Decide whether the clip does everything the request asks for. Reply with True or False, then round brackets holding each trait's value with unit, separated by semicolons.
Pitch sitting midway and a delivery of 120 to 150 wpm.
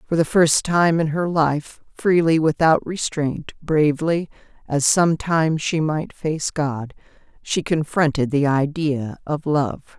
True (155 Hz; 140 wpm)